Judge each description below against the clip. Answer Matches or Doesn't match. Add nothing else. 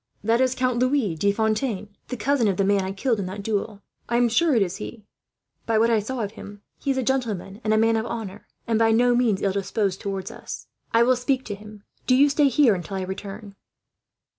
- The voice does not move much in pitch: Doesn't match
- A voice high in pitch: Matches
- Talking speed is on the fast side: Matches